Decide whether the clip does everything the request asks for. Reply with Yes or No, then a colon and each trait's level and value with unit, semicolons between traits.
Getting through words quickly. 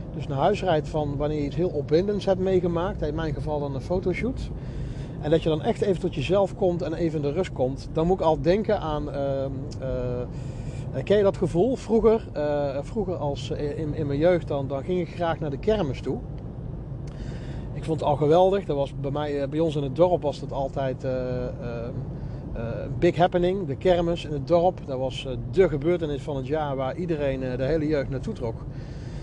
Yes: fast, 205 wpm